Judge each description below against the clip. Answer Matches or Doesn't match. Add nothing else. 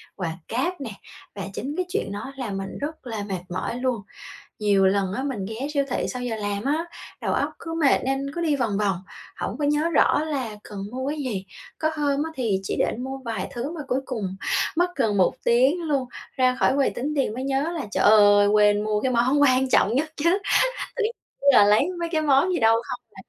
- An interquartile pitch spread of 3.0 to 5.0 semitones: Doesn't match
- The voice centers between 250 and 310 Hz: Matches